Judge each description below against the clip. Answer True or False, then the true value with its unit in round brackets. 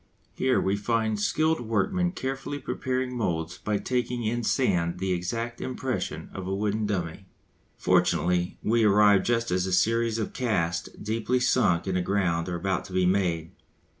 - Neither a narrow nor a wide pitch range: True (4.6 semitones)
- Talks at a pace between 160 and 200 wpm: True (165 wpm)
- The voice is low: True (105 Hz)